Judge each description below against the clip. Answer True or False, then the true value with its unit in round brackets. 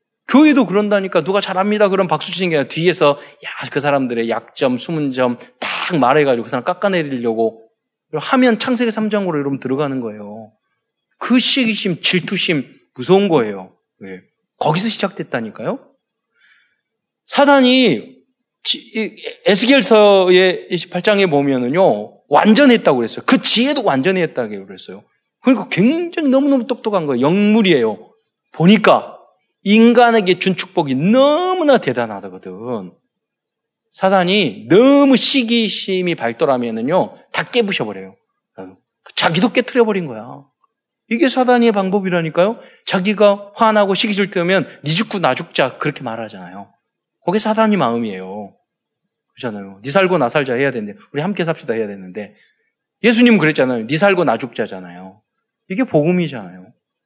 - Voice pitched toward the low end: False (190 Hz)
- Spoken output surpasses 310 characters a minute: True (320 characters per minute)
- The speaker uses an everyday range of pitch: False (8.4 semitones)